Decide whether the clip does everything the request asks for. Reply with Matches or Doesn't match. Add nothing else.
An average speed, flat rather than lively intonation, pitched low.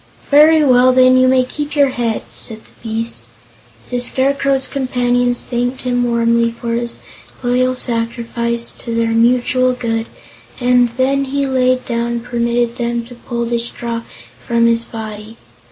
Doesn't match